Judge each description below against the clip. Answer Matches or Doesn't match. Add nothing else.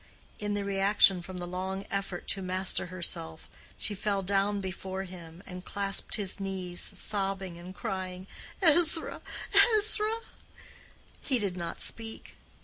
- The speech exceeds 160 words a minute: Doesn't match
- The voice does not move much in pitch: Matches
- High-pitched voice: Matches